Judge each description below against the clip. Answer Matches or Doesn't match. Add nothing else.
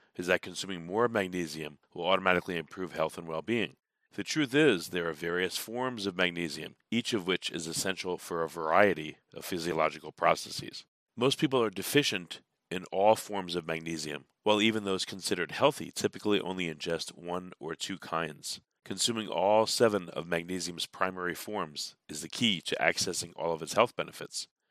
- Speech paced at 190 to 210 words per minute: Doesn't match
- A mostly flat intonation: Doesn't match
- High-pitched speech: Doesn't match